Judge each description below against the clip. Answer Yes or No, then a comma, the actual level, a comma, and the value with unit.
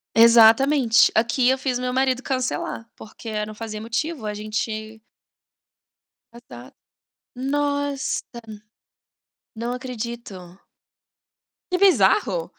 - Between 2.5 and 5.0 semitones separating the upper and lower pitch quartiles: Yes, average, 3.2 semitones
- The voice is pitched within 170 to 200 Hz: No, high, 240 Hz